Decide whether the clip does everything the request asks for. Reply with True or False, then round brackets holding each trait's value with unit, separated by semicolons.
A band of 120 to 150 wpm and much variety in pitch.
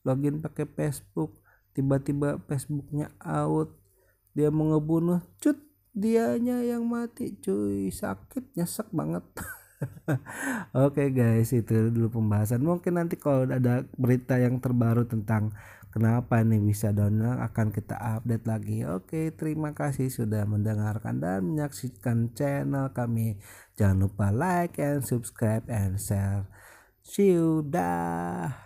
True (125 wpm; 5.9 semitones)